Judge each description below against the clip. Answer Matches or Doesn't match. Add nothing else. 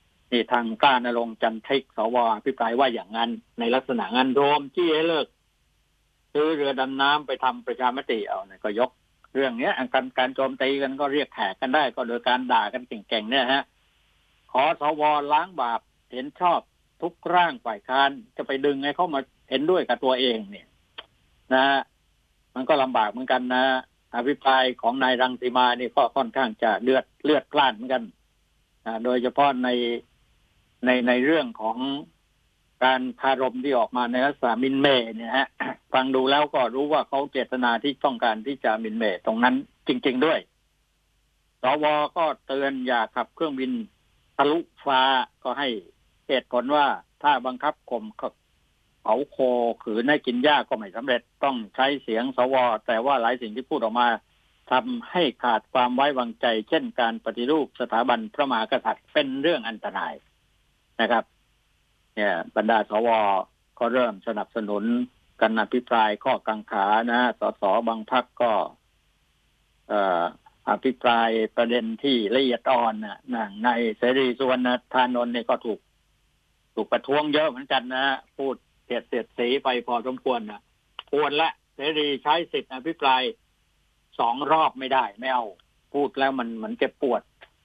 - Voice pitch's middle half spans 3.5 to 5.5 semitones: Doesn't match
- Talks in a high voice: Doesn't match